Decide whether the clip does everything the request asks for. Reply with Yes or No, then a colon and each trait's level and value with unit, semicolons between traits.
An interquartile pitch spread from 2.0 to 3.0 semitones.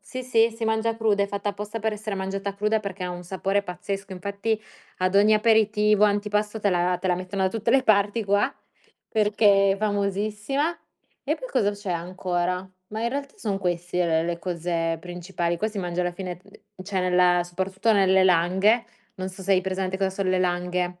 Yes: narrow, 2.6 semitones